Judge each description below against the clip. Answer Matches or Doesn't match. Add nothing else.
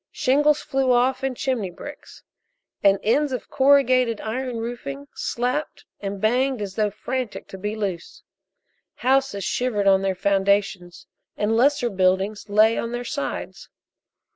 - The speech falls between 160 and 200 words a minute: Doesn't match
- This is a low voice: Doesn't match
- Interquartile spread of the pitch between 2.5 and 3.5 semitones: Doesn't match